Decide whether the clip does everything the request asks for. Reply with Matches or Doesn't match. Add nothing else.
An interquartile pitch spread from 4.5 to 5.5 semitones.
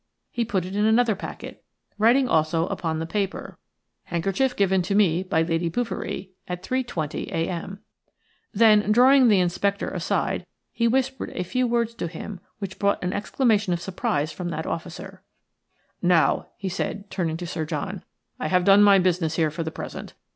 Doesn't match